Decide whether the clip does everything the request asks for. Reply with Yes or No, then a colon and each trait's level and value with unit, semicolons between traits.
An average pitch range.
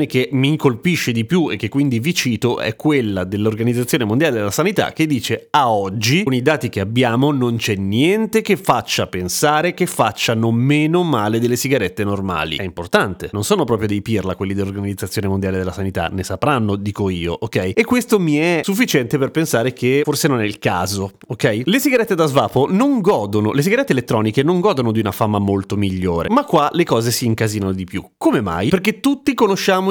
No: wide, 7.2 semitones